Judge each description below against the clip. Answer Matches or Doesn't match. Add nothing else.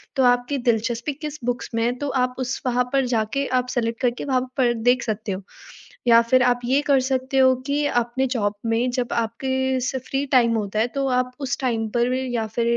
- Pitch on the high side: Matches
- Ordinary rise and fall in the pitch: Doesn't match